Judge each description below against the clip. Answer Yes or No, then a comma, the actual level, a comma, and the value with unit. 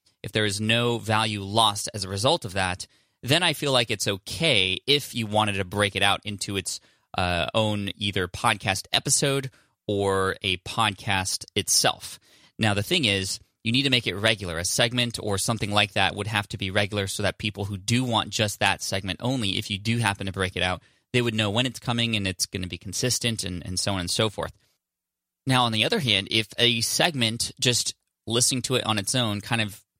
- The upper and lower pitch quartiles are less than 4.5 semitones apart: Yes, average, 3.1 semitones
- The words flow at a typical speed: No, fast, 220 wpm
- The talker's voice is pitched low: Yes, low, 105 Hz